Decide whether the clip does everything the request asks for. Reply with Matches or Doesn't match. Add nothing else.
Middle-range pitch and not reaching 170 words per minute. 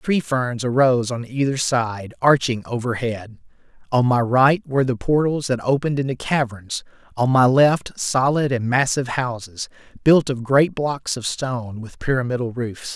Doesn't match